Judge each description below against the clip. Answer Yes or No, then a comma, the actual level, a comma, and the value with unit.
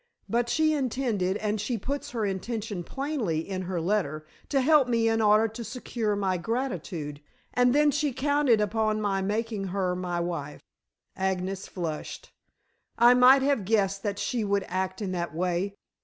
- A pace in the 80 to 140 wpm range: No, average, 165 wpm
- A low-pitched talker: No, high, 210 Hz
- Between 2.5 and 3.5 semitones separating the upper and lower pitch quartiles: No, average, 4.8 semitones